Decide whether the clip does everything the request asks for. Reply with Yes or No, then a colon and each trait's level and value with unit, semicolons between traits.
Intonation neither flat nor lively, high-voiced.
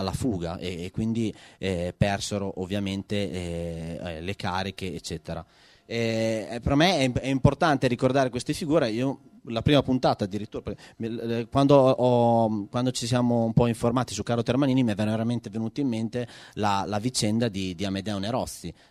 No: average, 4.3 semitones; low, 115 Hz